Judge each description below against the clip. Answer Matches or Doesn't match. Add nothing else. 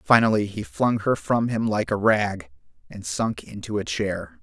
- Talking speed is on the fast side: Doesn't match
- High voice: Doesn't match